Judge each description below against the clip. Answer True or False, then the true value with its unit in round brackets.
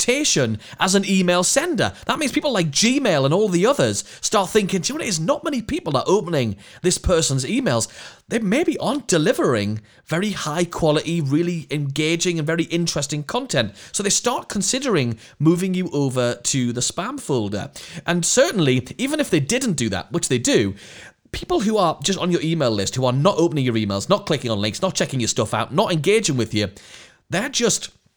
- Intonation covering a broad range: True (7.8 semitones)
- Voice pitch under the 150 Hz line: False (165 Hz)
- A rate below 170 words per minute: False (195 wpm)